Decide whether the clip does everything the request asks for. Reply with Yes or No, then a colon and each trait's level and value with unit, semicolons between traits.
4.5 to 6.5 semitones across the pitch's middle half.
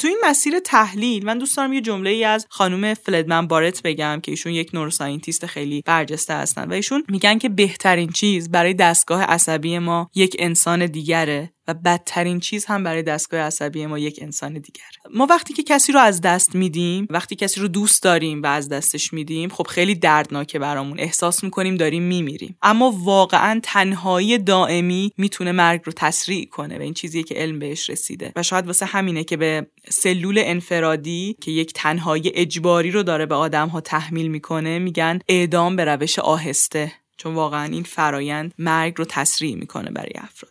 No: average, 3.5 semitones